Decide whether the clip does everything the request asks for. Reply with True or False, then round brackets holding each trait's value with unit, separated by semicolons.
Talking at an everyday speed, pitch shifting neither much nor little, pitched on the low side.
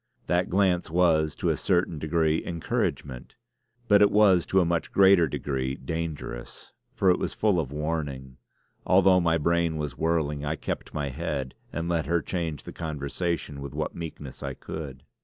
True (170 wpm; 3.1 semitones; 80 Hz)